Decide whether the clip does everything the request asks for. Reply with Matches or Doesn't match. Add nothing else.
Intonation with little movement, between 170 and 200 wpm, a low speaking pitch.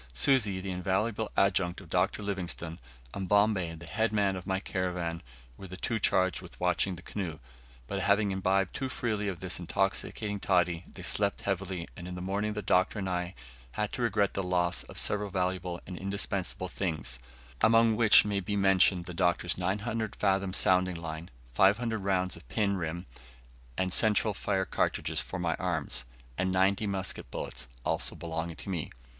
Matches